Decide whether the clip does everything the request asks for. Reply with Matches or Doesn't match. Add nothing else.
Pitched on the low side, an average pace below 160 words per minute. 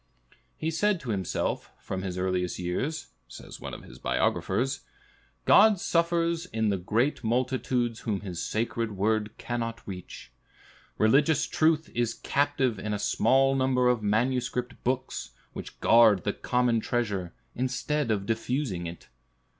Matches